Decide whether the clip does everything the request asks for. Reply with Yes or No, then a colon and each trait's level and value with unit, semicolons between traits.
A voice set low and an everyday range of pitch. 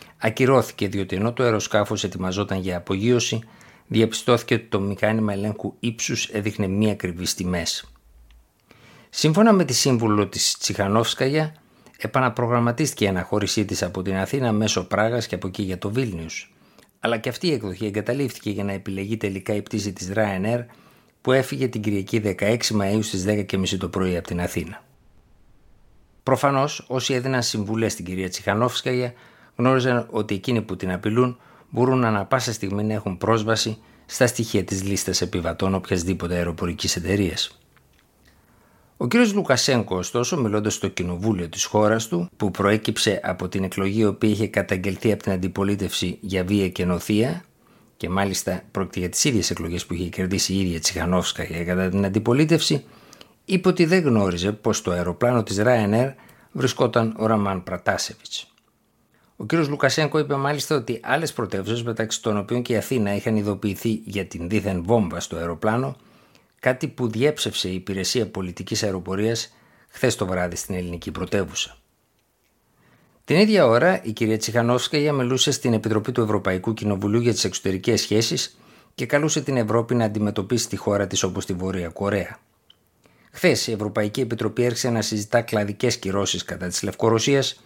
Yes: low, 105 Hz; average, 4.0 semitones